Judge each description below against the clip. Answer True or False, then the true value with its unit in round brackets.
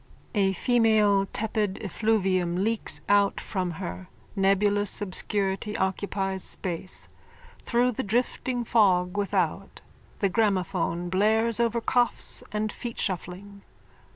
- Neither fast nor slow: False (100 wpm)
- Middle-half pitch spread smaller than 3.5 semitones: True (2.6 semitones)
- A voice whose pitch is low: False (200 Hz)